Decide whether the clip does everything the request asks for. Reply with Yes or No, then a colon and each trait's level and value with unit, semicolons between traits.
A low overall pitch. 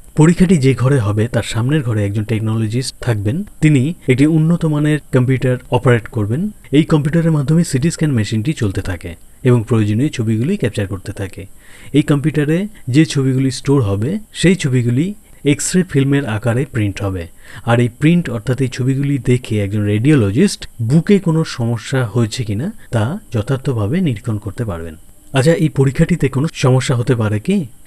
Yes: low, 130 Hz